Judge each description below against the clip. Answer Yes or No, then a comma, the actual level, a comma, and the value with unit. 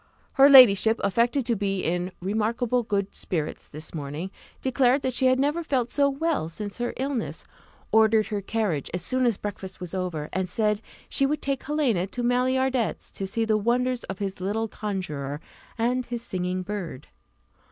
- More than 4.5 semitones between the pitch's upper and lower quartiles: Yes, average, 5.1 semitones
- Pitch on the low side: No, high, 220 Hz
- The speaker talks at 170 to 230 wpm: Yes, average, 175 wpm